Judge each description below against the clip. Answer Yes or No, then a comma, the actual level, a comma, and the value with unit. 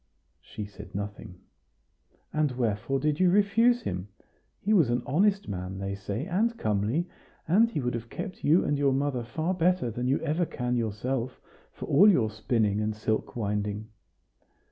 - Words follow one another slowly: No, average, 165 wpm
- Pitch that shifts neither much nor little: No, wide, 8.1 semitones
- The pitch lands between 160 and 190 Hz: No, low, 125 Hz